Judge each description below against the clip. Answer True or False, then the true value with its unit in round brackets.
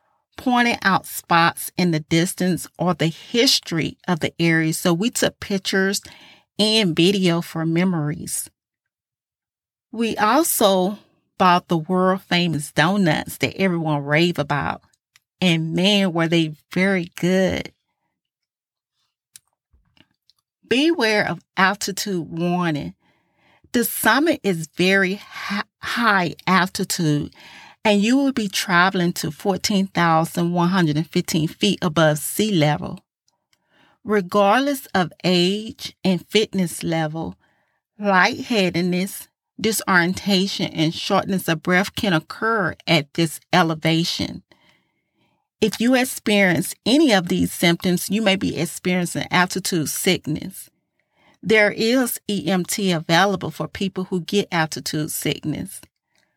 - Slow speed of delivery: True (105 wpm)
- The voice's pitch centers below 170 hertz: False (180 Hz)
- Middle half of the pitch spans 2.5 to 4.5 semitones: True (3.3 semitones)